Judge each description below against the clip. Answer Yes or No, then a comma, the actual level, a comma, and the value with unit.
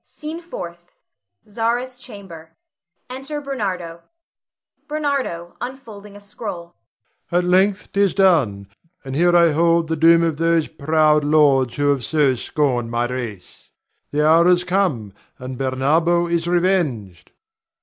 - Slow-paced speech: Yes, slow, 130 wpm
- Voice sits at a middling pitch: Yes, medium, 170 Hz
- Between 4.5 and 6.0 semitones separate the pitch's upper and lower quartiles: Yes, average, 5.2 semitones